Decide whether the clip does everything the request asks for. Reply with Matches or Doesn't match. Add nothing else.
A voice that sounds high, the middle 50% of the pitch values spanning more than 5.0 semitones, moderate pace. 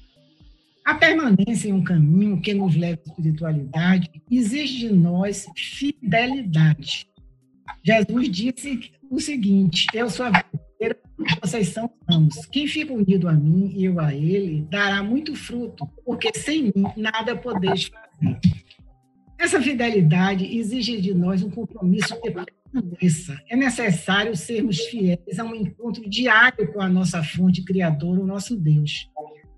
Matches